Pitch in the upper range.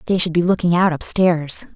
No: medium, 170 Hz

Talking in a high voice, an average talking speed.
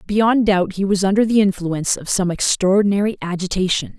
Yes: high, 195 Hz; average, 165 wpm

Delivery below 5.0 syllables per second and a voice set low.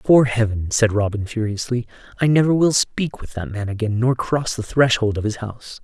No: 5.2 syllables/s; low, 115 Hz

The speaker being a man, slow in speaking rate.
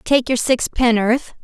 No: female; slow, 125 wpm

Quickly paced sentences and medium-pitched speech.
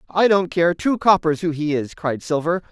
Yes: fast, 220 wpm; medium, 170 Hz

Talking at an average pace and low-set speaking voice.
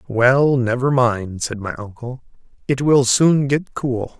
Yes: average, 155 wpm; low, 125 Hz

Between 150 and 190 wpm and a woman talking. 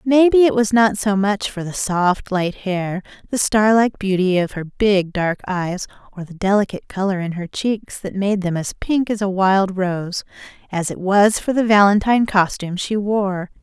No: average, 200 wpm; female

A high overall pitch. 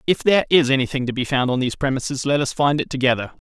No: low, 135 Hz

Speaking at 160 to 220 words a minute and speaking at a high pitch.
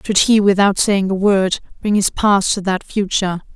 Yes: average, 200 wpm; high, 195 Hz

